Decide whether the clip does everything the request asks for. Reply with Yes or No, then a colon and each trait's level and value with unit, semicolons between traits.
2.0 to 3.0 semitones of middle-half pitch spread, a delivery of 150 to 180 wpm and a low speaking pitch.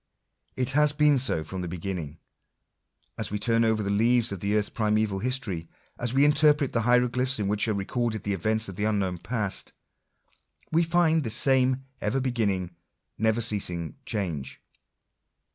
No: average, 4.5 semitones; average, 165 wpm; low, 110 Hz